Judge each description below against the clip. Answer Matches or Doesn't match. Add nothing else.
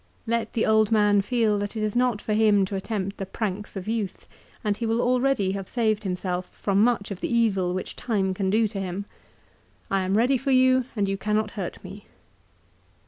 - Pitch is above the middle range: Matches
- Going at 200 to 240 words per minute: Matches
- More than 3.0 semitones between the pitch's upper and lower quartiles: Doesn't match